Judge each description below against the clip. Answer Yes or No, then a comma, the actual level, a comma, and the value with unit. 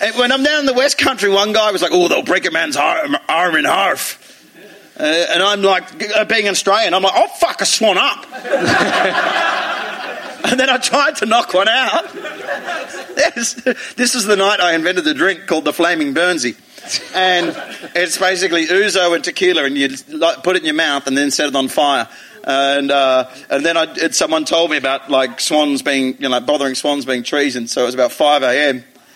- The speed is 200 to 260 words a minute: Yes, fast, 205 wpm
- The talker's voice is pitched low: No, medium, 180 Hz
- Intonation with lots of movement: Yes, wide, 8.7 semitones